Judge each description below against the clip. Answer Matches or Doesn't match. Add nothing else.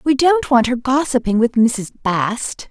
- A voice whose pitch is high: Matches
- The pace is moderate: Matches